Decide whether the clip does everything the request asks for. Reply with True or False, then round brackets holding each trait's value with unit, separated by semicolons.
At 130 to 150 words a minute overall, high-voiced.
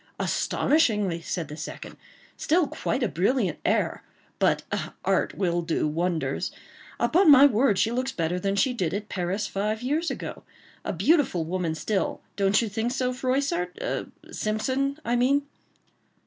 True (140 wpm; 215 Hz)